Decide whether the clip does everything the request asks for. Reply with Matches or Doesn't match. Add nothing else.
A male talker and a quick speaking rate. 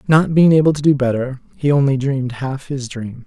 Matches